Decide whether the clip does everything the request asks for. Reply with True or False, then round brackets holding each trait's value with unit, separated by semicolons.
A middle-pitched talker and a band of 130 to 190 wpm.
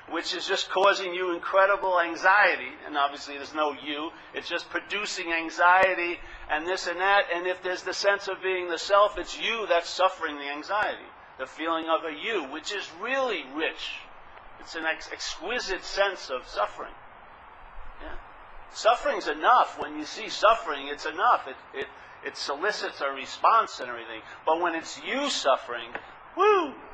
True (180 Hz; 165 wpm)